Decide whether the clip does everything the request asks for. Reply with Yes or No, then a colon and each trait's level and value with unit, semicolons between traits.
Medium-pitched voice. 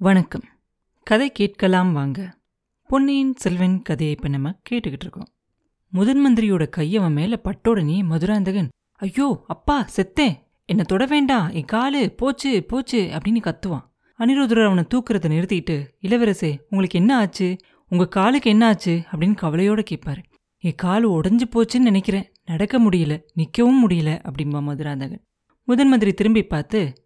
No: high, 195 Hz